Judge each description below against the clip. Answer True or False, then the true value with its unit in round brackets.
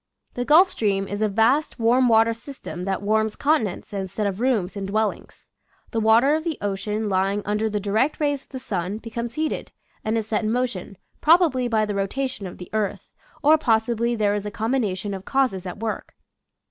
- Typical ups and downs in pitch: True (3.8 semitones)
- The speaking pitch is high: True (220 Hz)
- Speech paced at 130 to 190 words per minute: False (200 wpm)